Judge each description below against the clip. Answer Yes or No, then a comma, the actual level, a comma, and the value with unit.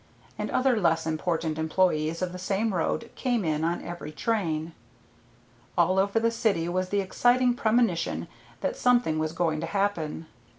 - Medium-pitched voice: Yes, medium, 180 Hz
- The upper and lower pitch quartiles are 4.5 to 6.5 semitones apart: Yes, average, 5.3 semitones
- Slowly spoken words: No, average, 160 wpm